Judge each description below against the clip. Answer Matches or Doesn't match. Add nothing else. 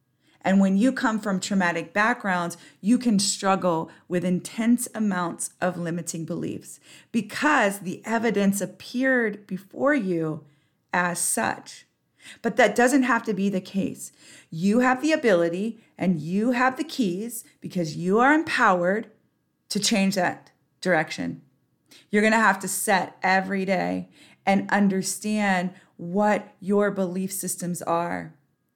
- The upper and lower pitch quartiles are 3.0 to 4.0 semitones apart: Matches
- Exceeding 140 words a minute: Doesn't match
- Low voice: Doesn't match